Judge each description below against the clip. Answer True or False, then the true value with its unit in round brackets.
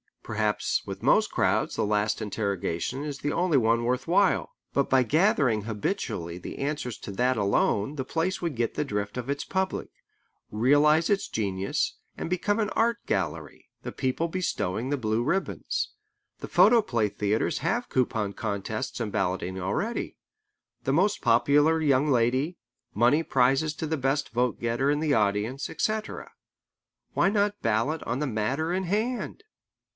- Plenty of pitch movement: True (6.8 semitones)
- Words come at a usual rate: True (155 wpm)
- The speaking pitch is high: False (130 Hz)